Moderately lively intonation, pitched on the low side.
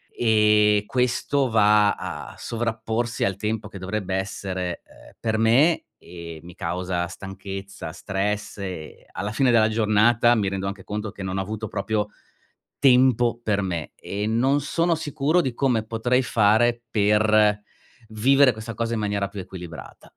Yes: average, 3.2 semitones; low, 105 Hz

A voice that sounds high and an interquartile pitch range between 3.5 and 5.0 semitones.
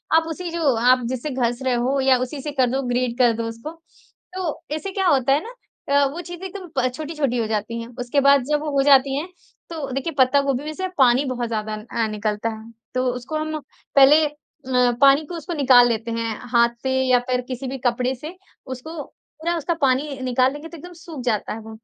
Yes: very high, 265 Hz; average, 4.0 semitones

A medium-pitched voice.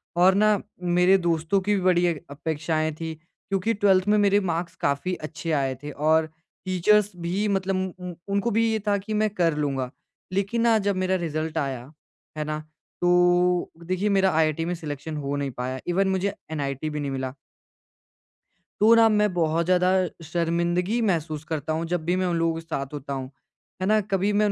Yes: medium, 175 Hz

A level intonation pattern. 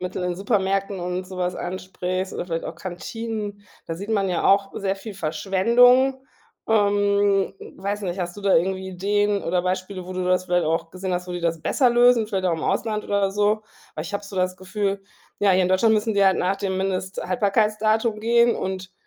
Yes: narrow, 2.1 semitones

